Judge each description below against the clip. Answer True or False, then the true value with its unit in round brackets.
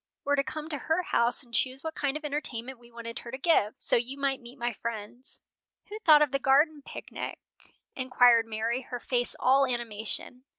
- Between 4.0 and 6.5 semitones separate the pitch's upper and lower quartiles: False (3.3 semitones)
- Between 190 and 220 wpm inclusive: True (200 wpm)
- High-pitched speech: True (255 Hz)